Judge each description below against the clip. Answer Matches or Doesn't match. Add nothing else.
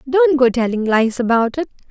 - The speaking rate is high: Doesn't match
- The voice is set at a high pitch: Matches